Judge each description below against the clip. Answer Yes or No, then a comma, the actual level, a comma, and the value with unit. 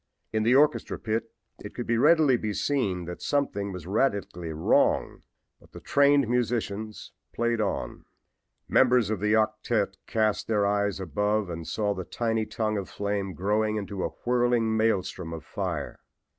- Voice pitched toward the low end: Yes, low, 110 Hz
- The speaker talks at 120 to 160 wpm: Yes, average, 155 wpm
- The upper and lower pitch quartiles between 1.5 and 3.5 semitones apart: Yes, average, 2.8 semitones